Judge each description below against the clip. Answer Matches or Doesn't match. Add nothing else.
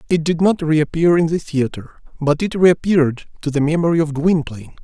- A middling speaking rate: Matches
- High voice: Doesn't match